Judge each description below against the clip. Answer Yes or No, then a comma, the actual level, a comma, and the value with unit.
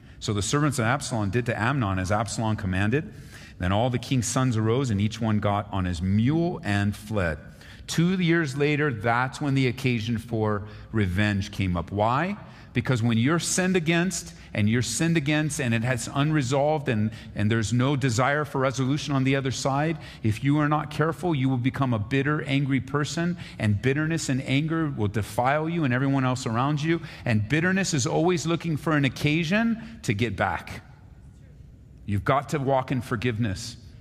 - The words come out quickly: No, average, 180 wpm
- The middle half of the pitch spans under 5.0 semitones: No, wide, 5.4 semitones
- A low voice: Yes, low, 130 Hz